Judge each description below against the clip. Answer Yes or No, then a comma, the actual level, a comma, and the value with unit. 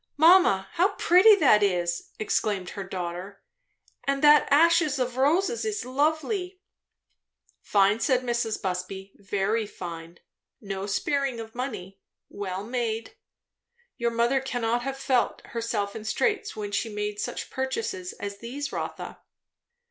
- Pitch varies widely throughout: Yes, wide, 6.1 semitones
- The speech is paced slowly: Yes, slow, 130 wpm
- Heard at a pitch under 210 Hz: No, high, 235 Hz